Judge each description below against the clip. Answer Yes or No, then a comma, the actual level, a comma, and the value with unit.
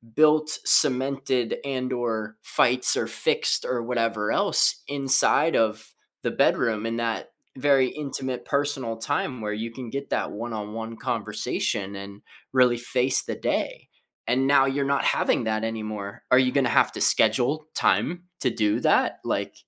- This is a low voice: Yes, low, 125 Hz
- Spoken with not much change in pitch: No, average, 3.3 semitones